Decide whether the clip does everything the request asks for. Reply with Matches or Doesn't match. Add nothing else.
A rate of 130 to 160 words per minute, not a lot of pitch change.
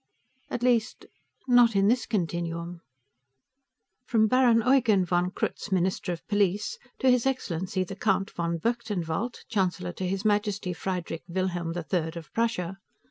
Doesn't match